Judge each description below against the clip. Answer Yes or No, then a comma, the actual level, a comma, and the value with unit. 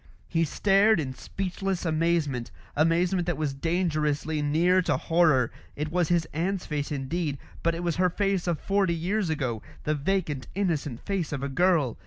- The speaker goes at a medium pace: Yes, average, 170 wpm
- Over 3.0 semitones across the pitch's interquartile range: Yes, average, 3.5 semitones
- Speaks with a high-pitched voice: No, medium, 165 Hz